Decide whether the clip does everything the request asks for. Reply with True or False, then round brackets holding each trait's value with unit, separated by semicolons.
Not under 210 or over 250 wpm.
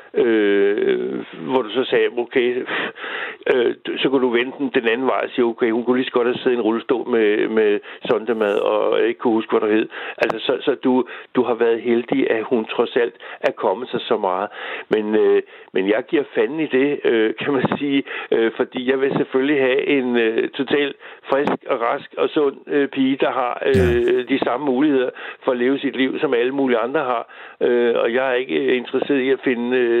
True (220 wpm)